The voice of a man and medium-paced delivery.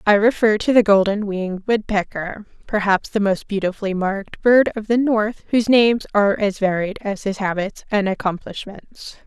No: female; average, 170 wpm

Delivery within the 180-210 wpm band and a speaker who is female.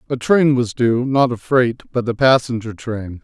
No: fast, 205 wpm; male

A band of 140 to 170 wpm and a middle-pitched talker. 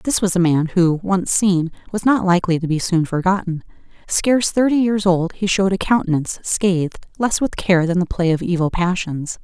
No: fast, 205 wpm; medium, 180 Hz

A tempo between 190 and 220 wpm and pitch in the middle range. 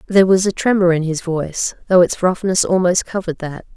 Yes: fast, 205 wpm; medium, 180 Hz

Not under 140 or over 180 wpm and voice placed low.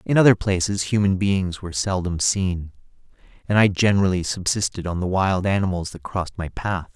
Yes: average, 175 wpm; very low, 95 Hz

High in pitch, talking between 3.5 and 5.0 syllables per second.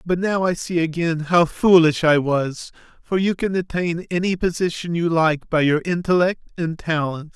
No: medium, 170 Hz; 4.6 syllables/s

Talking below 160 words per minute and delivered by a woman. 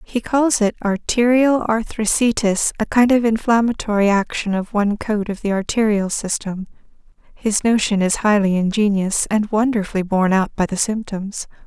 Yes: average, 145 wpm; female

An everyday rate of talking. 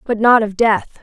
No: fast, 235 wpm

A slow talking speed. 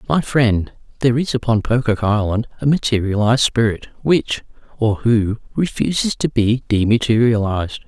Yes: slow, 130 wpm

